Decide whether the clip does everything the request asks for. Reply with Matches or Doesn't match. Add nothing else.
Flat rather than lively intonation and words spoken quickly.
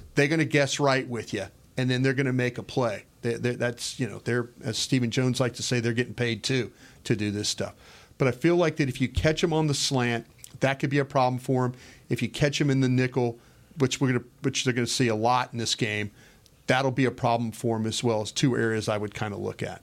Matches